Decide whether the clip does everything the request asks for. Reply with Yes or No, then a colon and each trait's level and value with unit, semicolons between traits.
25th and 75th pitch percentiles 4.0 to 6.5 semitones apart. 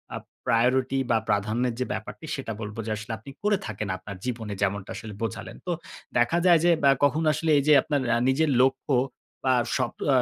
Yes: average, 4.7 semitones